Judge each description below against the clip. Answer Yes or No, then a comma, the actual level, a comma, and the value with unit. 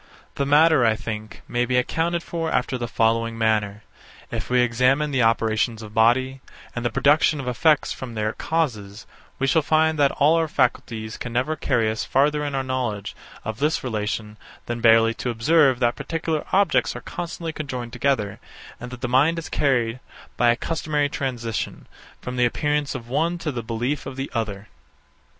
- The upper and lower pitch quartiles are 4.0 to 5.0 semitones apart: Yes, average, 4.5 semitones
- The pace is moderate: Yes, average, 180 wpm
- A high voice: No, low, 125 Hz